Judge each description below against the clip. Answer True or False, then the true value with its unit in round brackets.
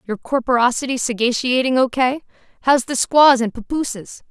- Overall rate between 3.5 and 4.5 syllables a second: False (5.1 syllables/s)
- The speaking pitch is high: True (250 Hz)